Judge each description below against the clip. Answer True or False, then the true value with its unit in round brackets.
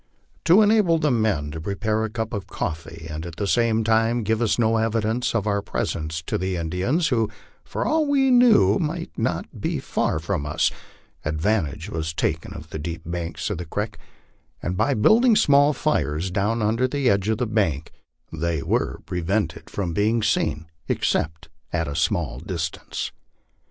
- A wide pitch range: True (6.2 semitones)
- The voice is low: True (105 Hz)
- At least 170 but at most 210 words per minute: True (175 wpm)